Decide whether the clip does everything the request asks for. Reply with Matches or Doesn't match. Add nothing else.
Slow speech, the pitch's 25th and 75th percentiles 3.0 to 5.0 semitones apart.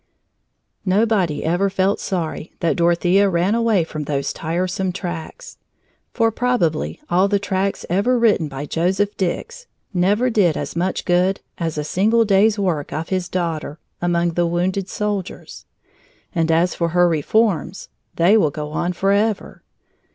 Doesn't match